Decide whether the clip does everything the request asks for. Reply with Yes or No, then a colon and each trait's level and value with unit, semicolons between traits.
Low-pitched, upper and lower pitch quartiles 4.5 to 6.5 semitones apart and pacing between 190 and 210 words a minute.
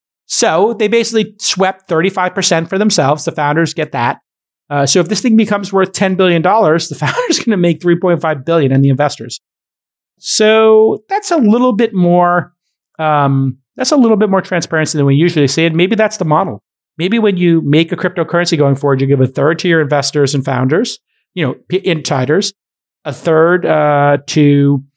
No: medium, 170 Hz; average, 4.9 semitones; average, 200 wpm